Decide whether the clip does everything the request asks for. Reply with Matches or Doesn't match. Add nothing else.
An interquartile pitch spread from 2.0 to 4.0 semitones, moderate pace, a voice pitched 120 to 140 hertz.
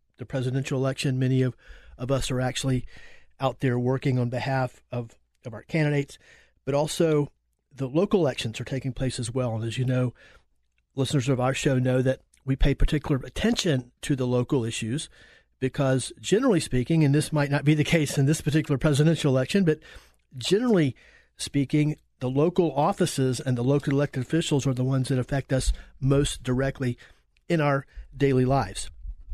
Matches